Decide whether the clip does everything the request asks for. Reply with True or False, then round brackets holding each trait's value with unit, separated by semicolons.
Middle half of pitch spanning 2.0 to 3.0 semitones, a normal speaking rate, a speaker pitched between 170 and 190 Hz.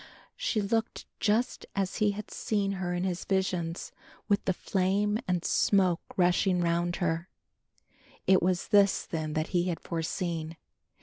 True (2.5 semitones; 145 wpm; 185 Hz)